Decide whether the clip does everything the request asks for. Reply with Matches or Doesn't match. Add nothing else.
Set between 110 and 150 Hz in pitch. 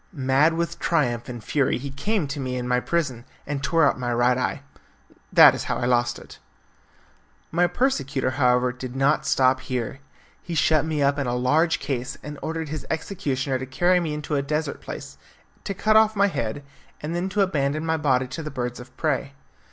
Matches